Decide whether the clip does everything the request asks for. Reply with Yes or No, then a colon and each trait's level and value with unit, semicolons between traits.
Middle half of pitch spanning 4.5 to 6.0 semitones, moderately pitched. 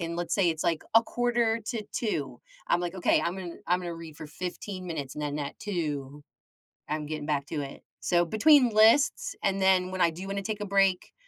Yes: average, 4.8 semitones; medium, 180 Hz